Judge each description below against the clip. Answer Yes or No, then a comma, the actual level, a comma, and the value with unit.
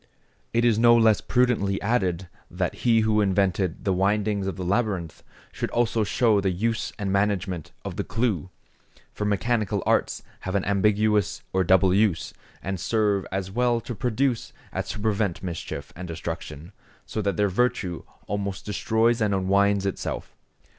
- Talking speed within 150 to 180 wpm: Yes, average, 160 wpm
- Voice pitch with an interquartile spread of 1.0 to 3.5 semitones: Yes, average, 2.9 semitones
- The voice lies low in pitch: Yes, low, 100 Hz